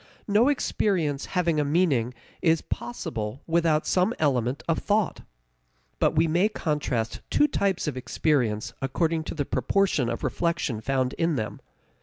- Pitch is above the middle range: No, medium, 155 Hz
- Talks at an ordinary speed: Yes, average, 145 wpm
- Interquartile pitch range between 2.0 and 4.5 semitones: No, wide, 5.4 semitones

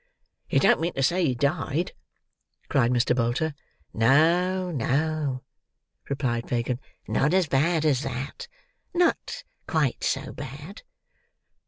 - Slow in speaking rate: Yes, slow, 120 wpm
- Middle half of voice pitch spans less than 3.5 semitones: No, average, 4.7 semitones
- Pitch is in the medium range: Yes, medium, 145 Hz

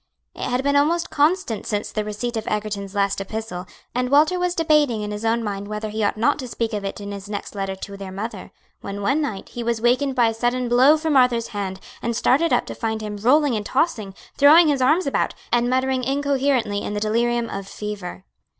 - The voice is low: No, high, 230 Hz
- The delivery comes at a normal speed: No, fast, 225 wpm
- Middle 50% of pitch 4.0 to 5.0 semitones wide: Yes, average, 4.6 semitones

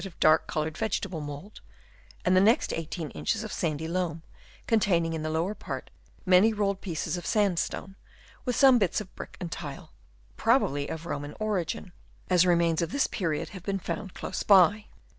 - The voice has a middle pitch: Yes, medium, 180 Hz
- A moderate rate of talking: Yes, average, 180 wpm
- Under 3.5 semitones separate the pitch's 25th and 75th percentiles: No, average, 4.0 semitones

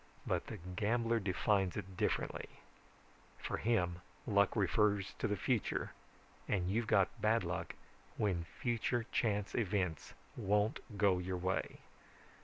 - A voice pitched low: Yes, low, 100 Hz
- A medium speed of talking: No, slow, 125 wpm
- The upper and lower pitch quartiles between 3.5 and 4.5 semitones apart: No, average, 3.1 semitones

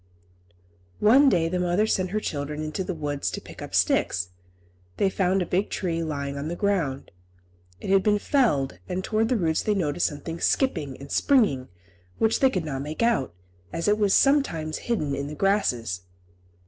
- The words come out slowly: No, average, 185 wpm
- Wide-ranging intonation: Yes, wide, 6.1 semitones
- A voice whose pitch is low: No, medium, 175 Hz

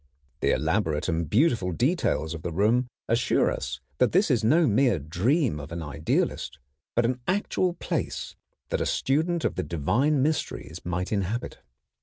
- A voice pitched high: No, low, 110 Hz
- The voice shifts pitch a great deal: Yes, wide, 8.9 semitones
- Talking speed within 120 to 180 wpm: Yes, average, 160 wpm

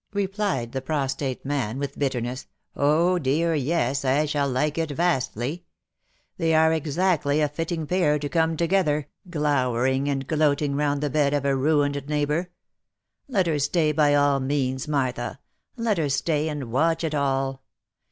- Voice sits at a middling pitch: Yes, medium, 145 Hz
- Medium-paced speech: Yes, average, 160 wpm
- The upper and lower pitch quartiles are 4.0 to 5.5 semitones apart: No, average, 2.9 semitones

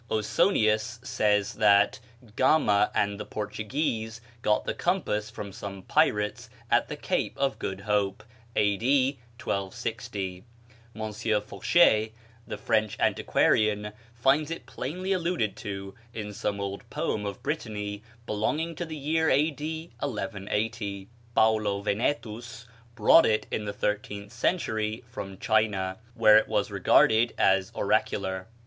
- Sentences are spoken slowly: Yes, slow, 125 wpm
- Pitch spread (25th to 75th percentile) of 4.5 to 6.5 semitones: No, average, 3.5 semitones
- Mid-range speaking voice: No, low, 110 Hz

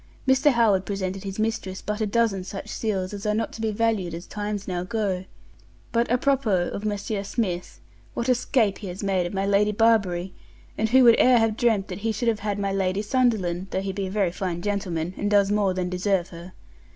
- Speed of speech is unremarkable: No, fast, 220 wpm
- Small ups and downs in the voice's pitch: No, average, 3.0 semitones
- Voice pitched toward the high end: Yes, high, 200 Hz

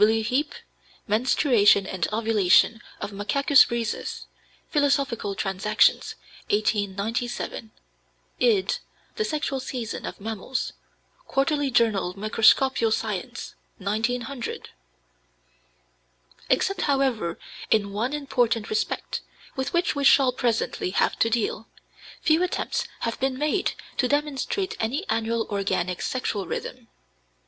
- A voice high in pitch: Yes, high, 230 Hz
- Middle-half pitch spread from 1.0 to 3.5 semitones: No, average, 4.4 semitones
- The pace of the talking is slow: Yes, slow, 105 wpm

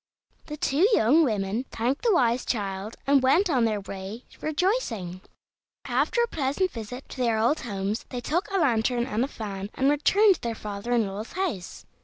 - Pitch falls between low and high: No, high, 240 Hz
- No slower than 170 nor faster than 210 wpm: Yes, average, 185 wpm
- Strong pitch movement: Yes, wide, 6.1 semitones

